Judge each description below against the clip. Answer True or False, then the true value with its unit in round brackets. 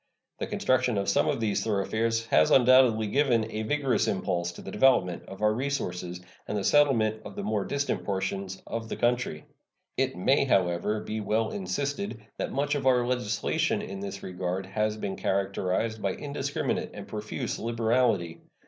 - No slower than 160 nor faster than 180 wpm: True (165 wpm)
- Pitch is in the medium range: False (110 Hz)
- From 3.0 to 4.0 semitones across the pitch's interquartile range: False (4.4 semitones)